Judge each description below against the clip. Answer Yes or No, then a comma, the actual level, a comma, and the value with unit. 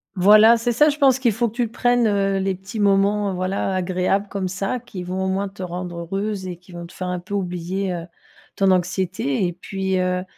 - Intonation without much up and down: Yes, narrow, 2.2 semitones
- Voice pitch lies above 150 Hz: Yes, high, 190 Hz